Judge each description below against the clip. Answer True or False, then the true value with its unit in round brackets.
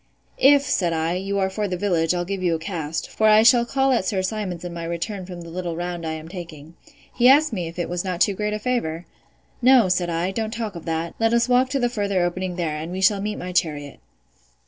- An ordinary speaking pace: False (250 wpm)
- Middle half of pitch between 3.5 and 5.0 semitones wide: True (4.0 semitones)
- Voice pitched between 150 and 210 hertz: True (185 Hz)